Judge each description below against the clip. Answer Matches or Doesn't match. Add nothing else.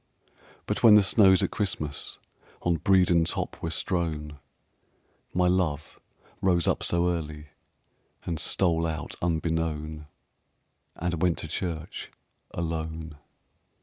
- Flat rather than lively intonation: Matches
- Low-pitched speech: Matches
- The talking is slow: Matches